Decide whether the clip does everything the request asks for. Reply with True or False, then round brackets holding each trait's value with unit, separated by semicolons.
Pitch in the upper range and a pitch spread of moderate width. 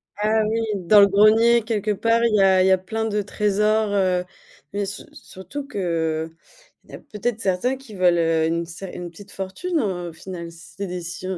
True (200 Hz; 3.2 semitones)